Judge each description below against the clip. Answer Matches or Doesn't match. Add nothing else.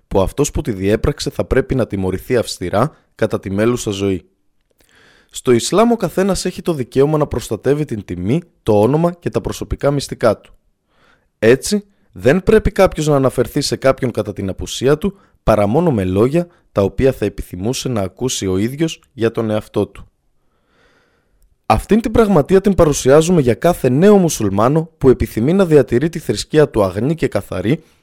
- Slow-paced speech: Doesn't match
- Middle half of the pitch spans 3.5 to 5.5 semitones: Doesn't match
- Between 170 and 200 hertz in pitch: Doesn't match